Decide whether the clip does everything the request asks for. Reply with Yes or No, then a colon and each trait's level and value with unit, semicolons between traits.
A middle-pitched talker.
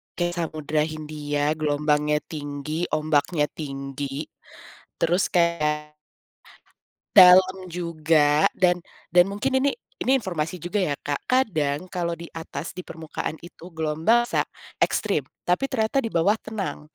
Yes: medium, 165 Hz